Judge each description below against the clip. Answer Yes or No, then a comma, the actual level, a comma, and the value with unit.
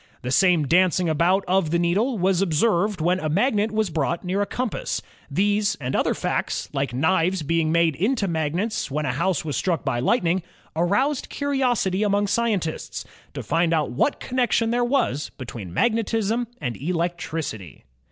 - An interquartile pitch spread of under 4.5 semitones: No, average, 5.0 semitones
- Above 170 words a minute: No, average, 160 wpm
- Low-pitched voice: No, medium, 180 Hz